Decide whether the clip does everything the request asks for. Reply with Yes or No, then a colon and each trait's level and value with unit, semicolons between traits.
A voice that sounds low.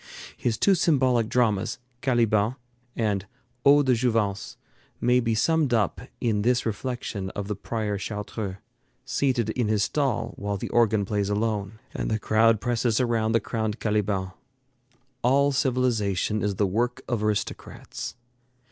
Yes: low, 110 Hz